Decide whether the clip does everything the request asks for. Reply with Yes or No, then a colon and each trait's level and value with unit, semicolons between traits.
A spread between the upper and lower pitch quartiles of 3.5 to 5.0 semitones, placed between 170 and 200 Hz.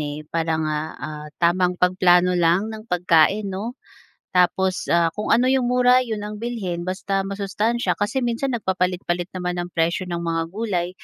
Yes: average, 3.8 semitones; medium, 185 Hz